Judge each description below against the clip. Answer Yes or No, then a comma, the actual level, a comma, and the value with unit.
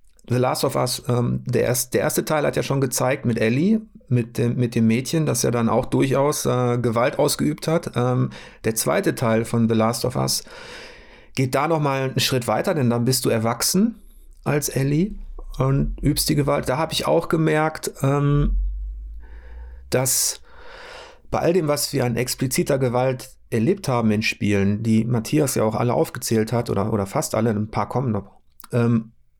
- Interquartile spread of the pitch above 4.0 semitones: Yes, average, 5.2 semitones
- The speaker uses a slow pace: No, fast, 190 wpm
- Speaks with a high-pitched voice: No, low, 125 Hz